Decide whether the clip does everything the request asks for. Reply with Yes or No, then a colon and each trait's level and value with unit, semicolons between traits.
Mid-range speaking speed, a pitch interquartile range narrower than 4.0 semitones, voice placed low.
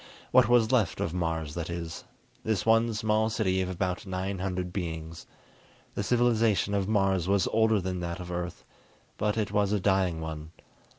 Yes: average, 175 wpm; average, 3.5 semitones; very low, 95 Hz